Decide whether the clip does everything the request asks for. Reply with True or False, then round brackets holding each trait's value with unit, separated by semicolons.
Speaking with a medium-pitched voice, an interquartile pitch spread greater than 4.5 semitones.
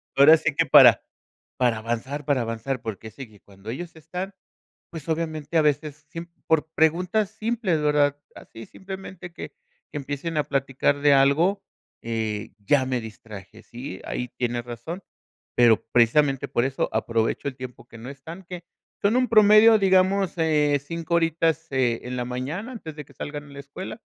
True (145 Hz; 5.4 semitones)